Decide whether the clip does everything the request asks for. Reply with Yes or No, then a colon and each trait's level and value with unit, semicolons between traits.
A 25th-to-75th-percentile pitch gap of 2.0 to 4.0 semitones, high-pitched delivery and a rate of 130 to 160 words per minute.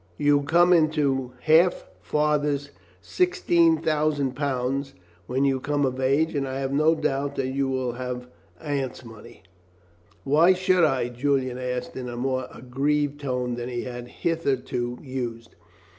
No: average, 2.9 semitones; low, 135 Hz; average, 140 wpm